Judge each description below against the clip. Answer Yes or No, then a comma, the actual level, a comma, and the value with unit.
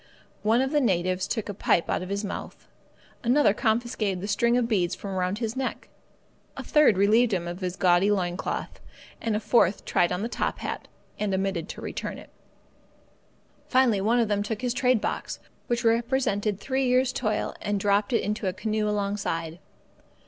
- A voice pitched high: Yes, high, 210 Hz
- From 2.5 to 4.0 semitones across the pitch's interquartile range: Yes, average, 3.7 semitones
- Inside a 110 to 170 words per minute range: No, average, 185 wpm